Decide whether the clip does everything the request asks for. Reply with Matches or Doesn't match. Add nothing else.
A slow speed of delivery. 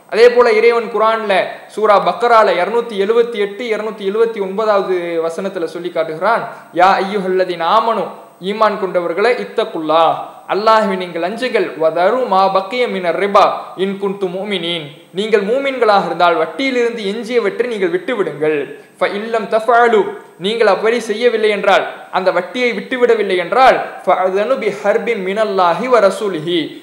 Matches